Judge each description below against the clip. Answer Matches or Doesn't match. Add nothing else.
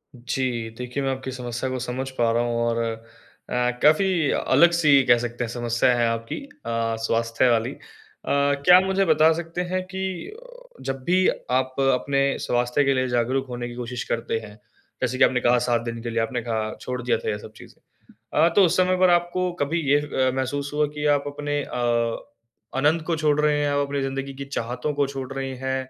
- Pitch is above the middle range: Doesn't match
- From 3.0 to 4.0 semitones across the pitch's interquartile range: Matches